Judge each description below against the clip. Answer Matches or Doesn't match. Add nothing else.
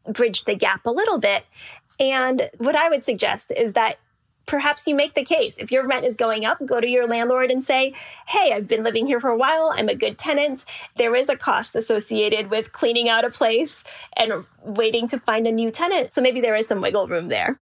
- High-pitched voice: Matches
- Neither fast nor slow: Doesn't match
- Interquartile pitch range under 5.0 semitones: Matches